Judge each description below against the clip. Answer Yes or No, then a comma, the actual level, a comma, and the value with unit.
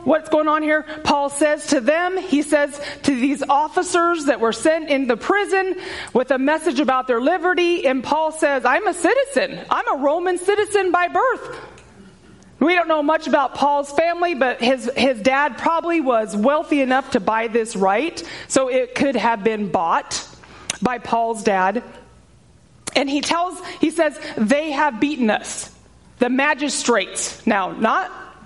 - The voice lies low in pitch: No, very high, 290 Hz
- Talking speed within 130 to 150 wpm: No, average, 165 wpm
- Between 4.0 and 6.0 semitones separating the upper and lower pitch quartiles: Yes, average, 4.4 semitones